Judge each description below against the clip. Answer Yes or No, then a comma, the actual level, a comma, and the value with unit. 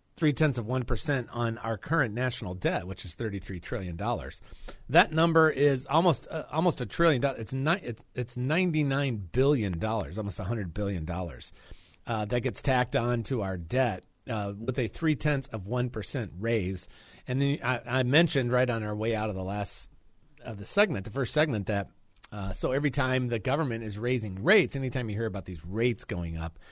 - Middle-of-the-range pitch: No, low, 120 Hz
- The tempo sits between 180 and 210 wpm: Yes, average, 200 wpm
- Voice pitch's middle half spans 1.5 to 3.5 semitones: No, average, 4.9 semitones